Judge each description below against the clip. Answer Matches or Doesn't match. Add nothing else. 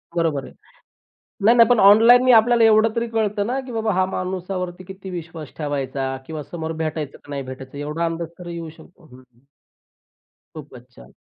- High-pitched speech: Doesn't match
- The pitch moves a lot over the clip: Matches